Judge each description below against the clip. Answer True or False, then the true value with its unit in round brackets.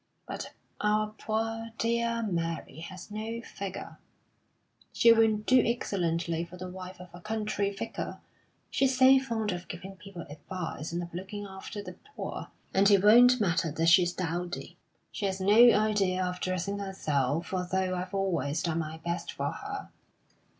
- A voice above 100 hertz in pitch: True (190 Hz)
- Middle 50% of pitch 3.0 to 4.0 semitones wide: True (3.6 semitones)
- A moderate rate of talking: True (155 wpm)